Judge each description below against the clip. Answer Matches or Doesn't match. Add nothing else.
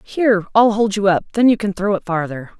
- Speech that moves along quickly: Matches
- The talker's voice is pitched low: Doesn't match